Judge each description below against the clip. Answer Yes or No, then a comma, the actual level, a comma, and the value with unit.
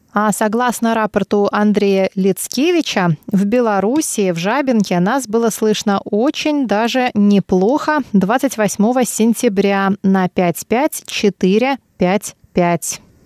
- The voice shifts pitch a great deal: No, average, 3.7 semitones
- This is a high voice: Yes, high, 210 Hz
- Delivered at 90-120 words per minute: Yes, slow, 110 wpm